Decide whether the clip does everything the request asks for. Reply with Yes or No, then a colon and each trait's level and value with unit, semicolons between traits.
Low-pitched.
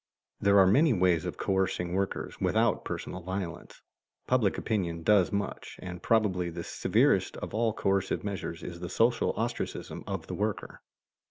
Yes: very low, 95 Hz